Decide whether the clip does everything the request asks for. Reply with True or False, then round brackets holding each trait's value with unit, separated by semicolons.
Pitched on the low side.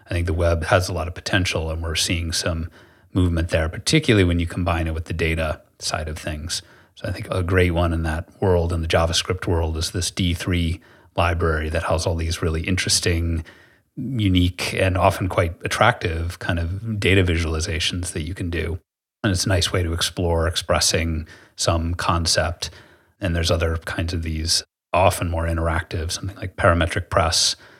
True (85 Hz)